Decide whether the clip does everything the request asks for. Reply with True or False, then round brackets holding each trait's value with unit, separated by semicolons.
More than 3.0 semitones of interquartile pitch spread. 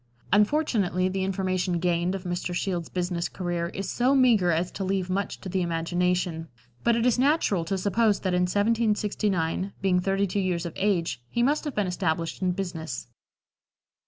False (2.6 semitones)